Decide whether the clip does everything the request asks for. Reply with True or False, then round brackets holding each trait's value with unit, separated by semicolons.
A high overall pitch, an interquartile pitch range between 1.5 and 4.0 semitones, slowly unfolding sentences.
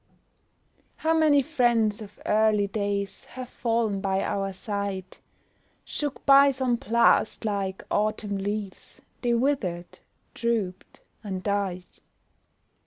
True (210 Hz; 3.4 semitones; 105 wpm)